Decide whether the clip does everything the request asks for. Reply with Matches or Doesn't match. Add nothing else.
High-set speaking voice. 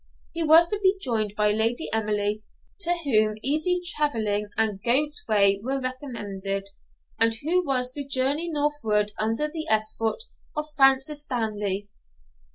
Matches